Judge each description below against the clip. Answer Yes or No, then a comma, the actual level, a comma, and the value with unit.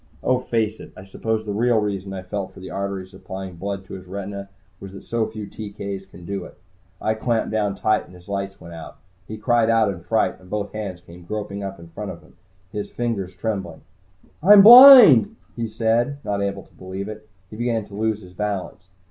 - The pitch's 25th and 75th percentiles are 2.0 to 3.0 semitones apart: Yes, narrow, 2.6 semitones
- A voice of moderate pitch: No, low, 100 Hz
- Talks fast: Yes, fast, 215 wpm